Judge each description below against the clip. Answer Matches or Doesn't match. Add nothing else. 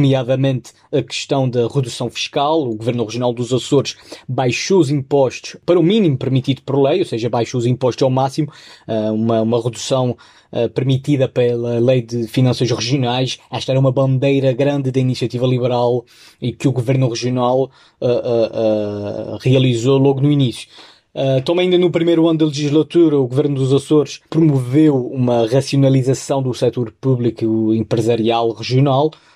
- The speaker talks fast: Doesn't match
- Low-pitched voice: Matches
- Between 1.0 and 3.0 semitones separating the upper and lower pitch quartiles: Matches